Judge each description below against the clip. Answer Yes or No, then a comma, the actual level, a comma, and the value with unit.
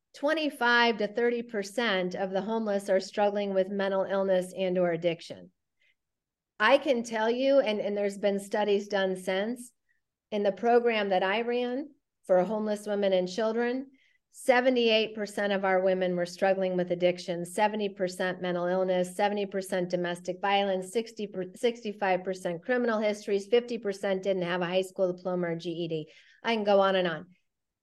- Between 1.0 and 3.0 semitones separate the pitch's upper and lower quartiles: No, average, 3.4 semitones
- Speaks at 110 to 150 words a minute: No, average, 160 wpm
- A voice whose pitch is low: No, high, 200 Hz